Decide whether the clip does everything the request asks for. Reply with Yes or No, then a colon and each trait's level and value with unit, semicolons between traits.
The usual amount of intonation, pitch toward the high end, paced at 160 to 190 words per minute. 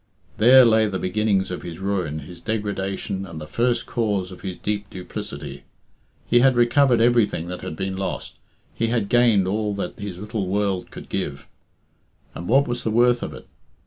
No: average, 4.1 semitones; low, 100 Hz; average, 180 wpm